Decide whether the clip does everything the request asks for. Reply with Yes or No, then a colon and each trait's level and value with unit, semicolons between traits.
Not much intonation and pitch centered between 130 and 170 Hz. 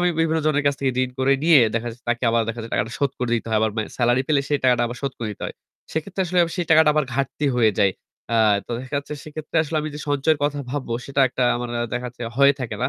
No: average, 4.0 semitones; low, 135 Hz